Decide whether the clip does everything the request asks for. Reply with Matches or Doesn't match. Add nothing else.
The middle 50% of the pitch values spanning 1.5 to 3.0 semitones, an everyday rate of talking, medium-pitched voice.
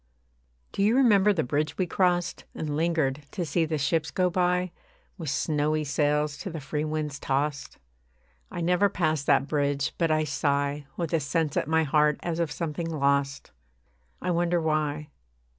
Matches